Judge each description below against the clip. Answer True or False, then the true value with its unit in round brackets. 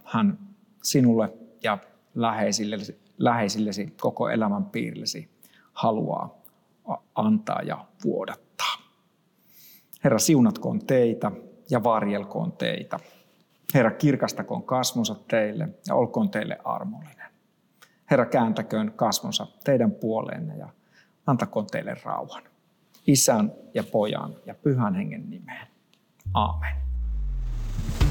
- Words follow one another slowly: True (90 wpm)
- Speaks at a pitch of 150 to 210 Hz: False (140 Hz)